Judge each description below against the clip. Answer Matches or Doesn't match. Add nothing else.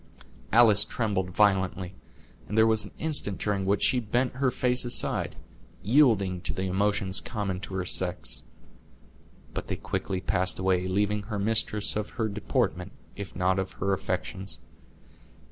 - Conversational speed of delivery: Matches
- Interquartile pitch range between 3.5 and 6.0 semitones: Doesn't match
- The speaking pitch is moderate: Doesn't match